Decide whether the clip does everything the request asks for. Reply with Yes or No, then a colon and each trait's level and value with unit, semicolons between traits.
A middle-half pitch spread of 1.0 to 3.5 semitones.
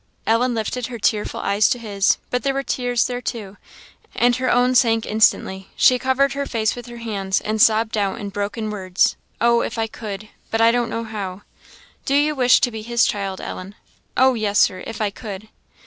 Yes: average, 3.0 semitones